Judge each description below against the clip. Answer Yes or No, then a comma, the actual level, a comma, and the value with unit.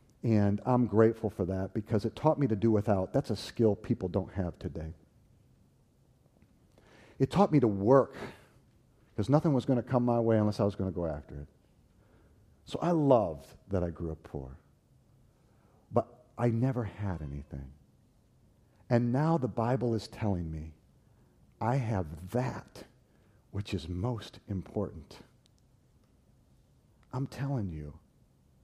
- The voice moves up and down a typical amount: Yes, average, 5.0 semitones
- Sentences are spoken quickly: No, average, 145 wpm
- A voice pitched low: Yes, low, 110 Hz